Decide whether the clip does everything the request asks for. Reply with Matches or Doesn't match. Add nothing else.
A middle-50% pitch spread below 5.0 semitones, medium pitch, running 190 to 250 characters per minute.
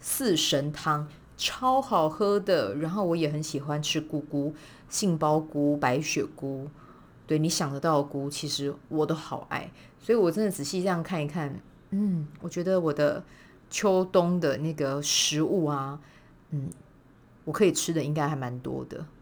Matches